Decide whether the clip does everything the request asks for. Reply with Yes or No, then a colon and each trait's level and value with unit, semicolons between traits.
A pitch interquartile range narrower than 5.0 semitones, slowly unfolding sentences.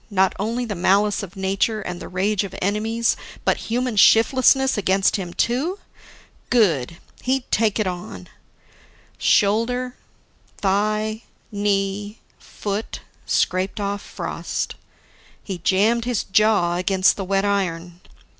Yes: average, 2.7 semitones; slow, 120 wpm